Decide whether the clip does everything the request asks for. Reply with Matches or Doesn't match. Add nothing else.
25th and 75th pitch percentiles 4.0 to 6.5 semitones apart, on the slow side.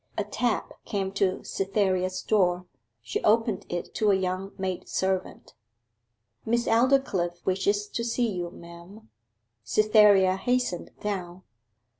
Doesn't match